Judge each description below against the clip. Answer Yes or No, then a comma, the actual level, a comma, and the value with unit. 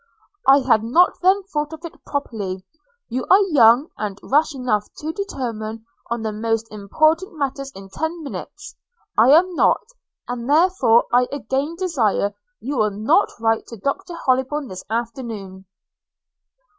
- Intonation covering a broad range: Yes, wide, 5.9 semitones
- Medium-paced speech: Yes, average, 150 wpm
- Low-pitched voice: No, very high, 255 Hz